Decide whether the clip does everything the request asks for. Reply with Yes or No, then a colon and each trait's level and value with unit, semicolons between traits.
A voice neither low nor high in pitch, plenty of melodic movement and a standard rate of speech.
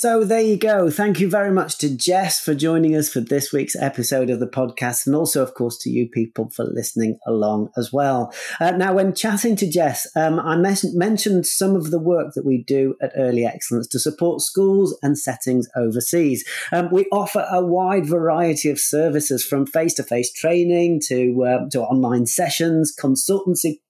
Yes: medium, 155 Hz; wide, 5.9 semitones; average, 190 wpm